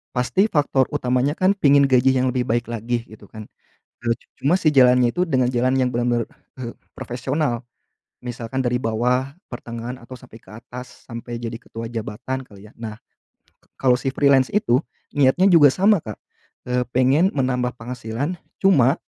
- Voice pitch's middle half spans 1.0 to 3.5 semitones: Yes, narrow, 2.4 semitones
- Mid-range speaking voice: No, low, 125 Hz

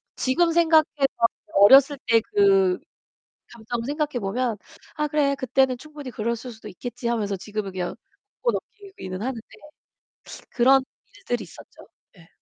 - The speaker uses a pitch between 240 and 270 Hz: Yes, very high, 255 Hz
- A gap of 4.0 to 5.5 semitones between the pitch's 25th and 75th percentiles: Yes, average, 5.1 semitones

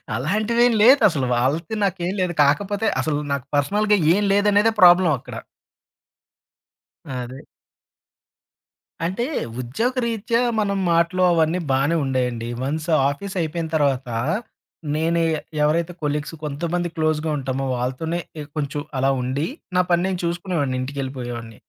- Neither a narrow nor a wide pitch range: No, wide, 5.8 semitones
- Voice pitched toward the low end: No, medium, 160 Hz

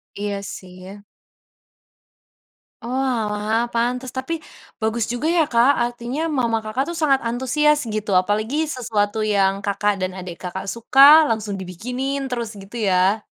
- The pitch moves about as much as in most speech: Yes, average, 3.6 semitones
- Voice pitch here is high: Yes, high, 225 Hz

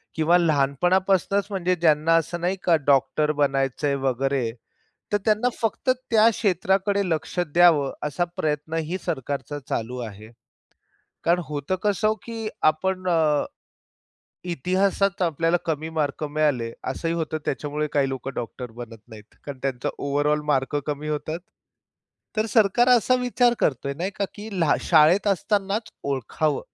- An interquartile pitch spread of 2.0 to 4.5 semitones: No, average, 5.1 semitones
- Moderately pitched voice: Yes, medium, 155 Hz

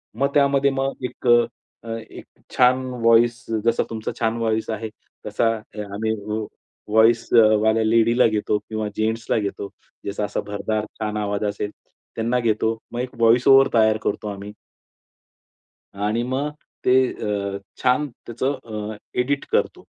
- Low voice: Yes, low, 110 Hz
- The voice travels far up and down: No, narrow, 2.4 semitones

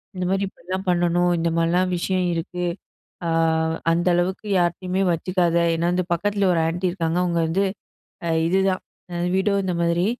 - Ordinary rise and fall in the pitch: No, narrow, 1.6 semitones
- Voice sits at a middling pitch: Yes, medium, 180 Hz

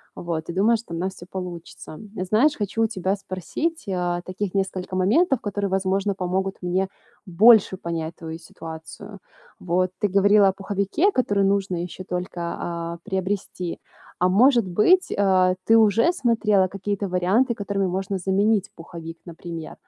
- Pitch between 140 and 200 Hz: Yes, high, 190 Hz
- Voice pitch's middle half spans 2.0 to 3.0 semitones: Yes, narrow, 2.5 semitones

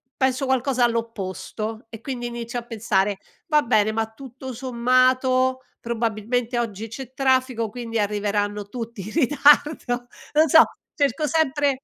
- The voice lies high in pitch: Yes, high, 240 Hz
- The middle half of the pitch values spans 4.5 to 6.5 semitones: No, average, 2.8 semitones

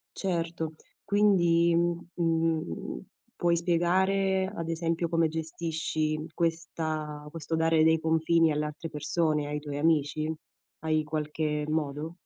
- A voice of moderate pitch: Yes, medium, 160 Hz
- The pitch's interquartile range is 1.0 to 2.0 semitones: Yes, narrow, 1.7 semitones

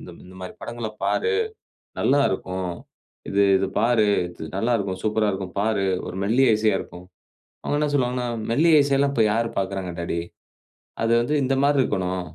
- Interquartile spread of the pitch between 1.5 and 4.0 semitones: No, average, 5.2 semitones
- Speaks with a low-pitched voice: Yes, low, 110 Hz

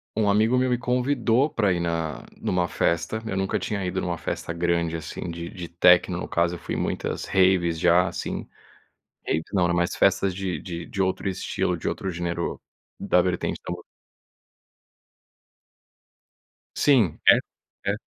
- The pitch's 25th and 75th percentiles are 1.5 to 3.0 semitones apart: Yes, narrow, 2.5 semitones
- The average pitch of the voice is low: Yes, very low, 90 Hz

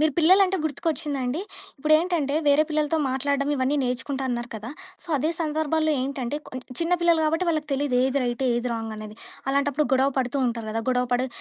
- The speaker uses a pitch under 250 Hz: No, very high, 280 Hz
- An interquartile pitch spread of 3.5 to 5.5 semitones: Yes, average, 3.8 semitones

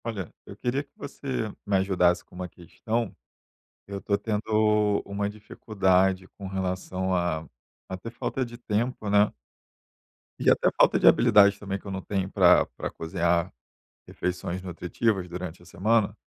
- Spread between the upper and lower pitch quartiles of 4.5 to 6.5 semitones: No, average, 2.7 semitones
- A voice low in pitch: Yes, low, 100 Hz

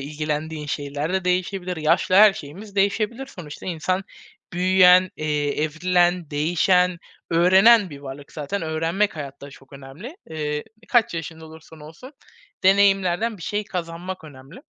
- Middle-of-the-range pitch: Yes, medium, 170 Hz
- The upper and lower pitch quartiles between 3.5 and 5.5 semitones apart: Yes, average, 3.9 semitones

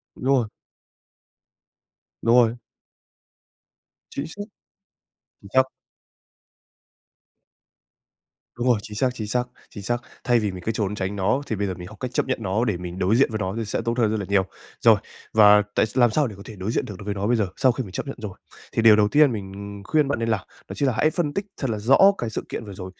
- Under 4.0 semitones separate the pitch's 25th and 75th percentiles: Yes, average, 3.5 semitones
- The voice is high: No, low, 110 Hz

